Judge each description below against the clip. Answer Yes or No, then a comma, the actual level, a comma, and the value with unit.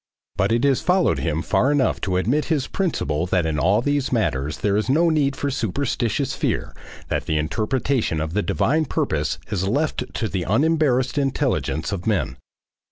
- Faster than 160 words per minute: Yes, average, 175 wpm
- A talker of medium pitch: No, low, 115 Hz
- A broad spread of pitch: Yes, wide, 7.7 semitones